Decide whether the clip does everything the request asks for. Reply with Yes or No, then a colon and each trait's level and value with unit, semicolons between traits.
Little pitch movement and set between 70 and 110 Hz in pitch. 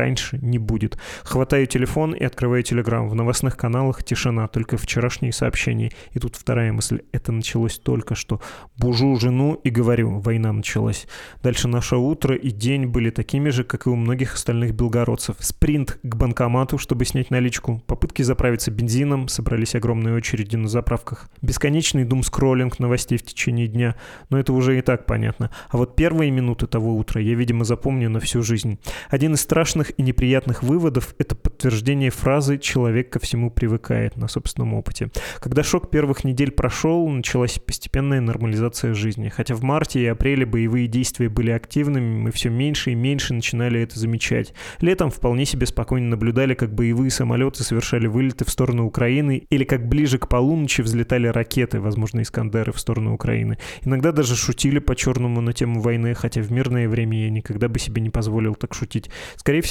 No: narrow, 2.2 semitones; low, 120 Hz